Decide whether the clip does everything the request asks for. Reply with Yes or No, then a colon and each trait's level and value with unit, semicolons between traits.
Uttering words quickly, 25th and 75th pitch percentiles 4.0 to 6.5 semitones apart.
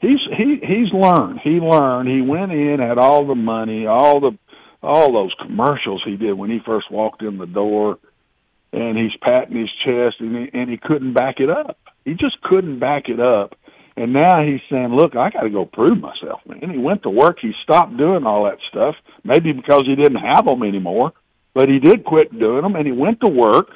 Yes: fast, 215 wpm; average, 5.1 semitones